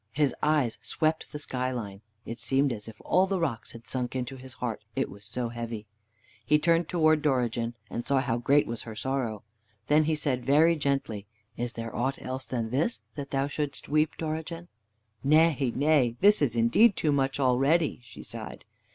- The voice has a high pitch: No, low, 135 Hz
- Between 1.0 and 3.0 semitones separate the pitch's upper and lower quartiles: No, average, 4.4 semitones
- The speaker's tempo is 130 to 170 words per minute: No, average, 185 wpm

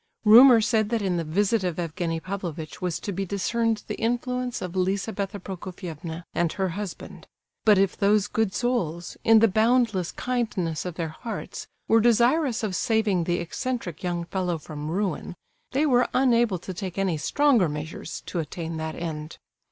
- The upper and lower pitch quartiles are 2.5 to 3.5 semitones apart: No, average, 4.8 semitones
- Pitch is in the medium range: No, high, 195 Hz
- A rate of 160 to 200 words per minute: Yes, average, 165 wpm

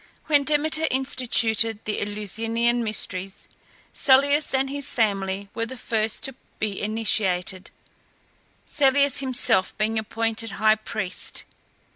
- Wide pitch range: No, average, 4.1 semitones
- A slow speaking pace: Yes, slow, 110 wpm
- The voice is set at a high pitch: Yes, high, 225 Hz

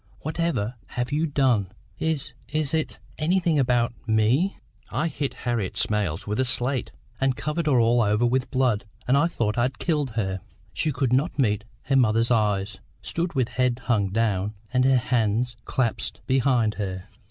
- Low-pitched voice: Yes, low, 125 Hz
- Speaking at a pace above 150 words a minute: Yes, average, 170 wpm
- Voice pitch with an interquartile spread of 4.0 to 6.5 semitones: Yes, average, 4.5 semitones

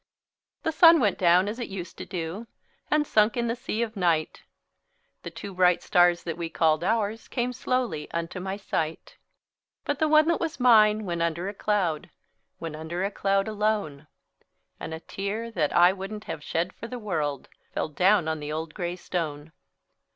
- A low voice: No, high, 190 Hz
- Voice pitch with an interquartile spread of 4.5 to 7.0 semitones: Yes, average, 4.8 semitones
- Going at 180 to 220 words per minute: Yes, average, 185 wpm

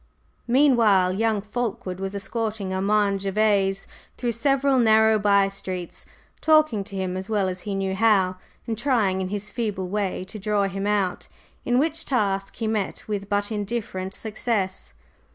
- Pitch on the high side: Yes, high, 205 Hz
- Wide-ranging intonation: No, narrow, 2.5 semitones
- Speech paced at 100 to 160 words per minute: Yes, average, 155 wpm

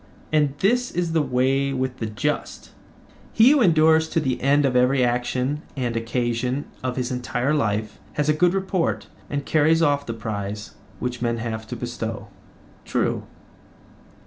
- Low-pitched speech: Yes, low, 130 Hz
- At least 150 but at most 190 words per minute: Yes, average, 160 wpm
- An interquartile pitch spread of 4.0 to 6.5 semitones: Yes, average, 4.4 semitones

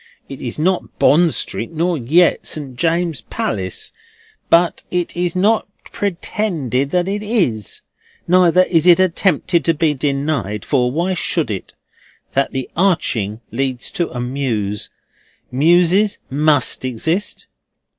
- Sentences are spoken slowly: Yes, slow, 125 wpm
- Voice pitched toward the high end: No, medium, 160 Hz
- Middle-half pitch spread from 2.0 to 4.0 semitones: No, wide, 5.5 semitones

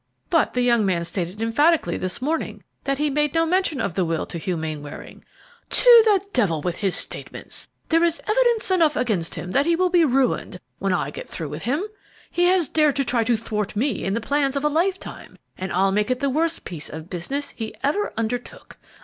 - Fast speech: Yes, fast, 215 wpm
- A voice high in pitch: Yes, very high, 250 Hz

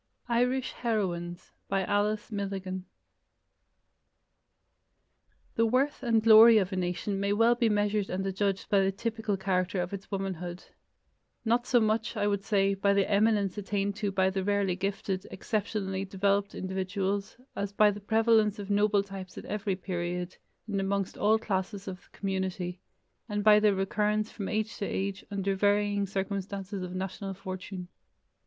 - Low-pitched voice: No, high, 200 Hz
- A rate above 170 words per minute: No, average, 155 wpm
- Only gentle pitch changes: Yes, narrow, 1.7 semitones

